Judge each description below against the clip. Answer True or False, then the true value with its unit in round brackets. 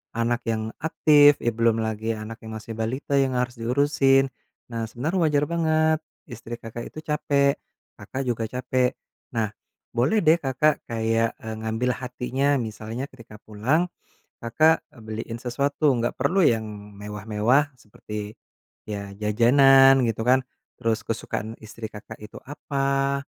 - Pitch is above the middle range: False (120 Hz)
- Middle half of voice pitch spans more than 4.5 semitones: False (3.7 semitones)